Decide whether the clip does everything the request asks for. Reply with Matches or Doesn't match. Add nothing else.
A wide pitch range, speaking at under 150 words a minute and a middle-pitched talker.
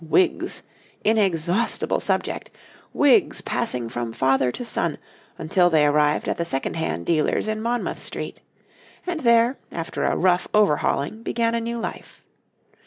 Matches